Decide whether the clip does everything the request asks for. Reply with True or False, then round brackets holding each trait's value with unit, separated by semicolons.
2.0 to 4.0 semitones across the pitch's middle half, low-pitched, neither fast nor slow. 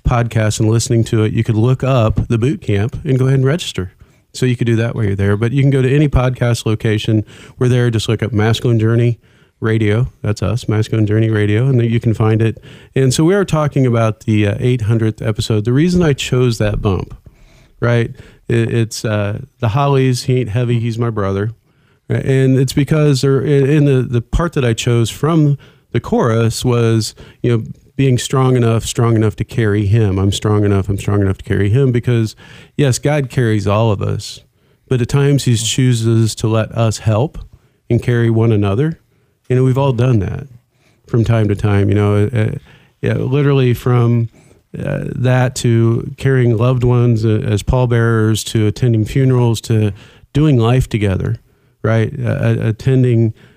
True (3.1 semitones; 120 Hz; 185 wpm)